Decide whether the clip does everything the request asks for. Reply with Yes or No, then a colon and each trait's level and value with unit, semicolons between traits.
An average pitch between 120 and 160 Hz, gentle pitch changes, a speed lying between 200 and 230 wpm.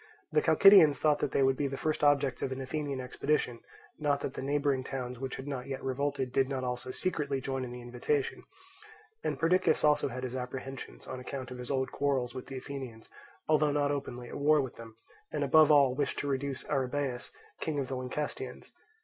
Yes: low, 135 Hz; narrow, 2.1 semitones; fast, 205 wpm